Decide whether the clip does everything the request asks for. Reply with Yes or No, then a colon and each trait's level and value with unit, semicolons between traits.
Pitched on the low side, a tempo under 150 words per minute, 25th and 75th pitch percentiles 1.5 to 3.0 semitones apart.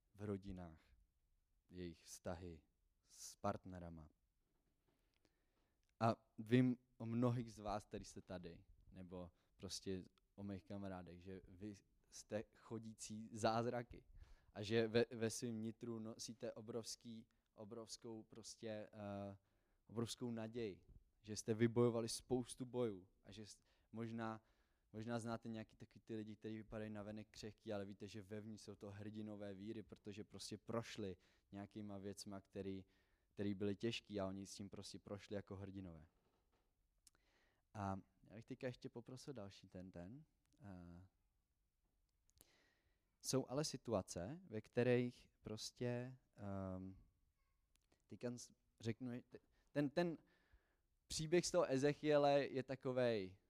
No: low, 105 Hz; average, 120 wpm; average, 3.4 semitones